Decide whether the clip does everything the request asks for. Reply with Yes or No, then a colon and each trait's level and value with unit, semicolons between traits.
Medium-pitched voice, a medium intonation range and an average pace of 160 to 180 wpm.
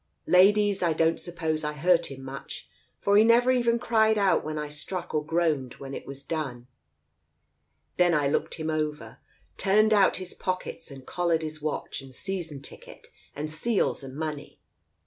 Yes: medium, 160 Hz; average, 4.4 semitones; average, 170 wpm